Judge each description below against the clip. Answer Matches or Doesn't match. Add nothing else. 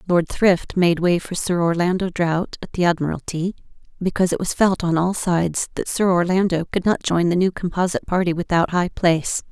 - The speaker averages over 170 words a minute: Matches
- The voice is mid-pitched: Matches